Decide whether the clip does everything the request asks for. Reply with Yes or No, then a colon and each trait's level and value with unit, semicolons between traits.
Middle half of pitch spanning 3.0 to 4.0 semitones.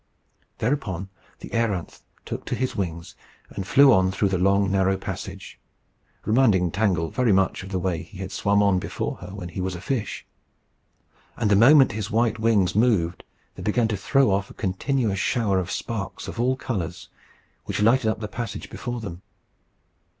Yes: average, 3.6 semitones